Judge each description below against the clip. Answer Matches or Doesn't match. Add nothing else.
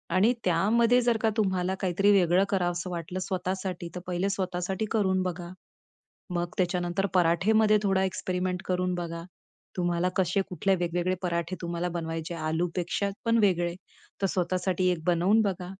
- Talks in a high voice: Doesn't match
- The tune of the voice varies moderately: Doesn't match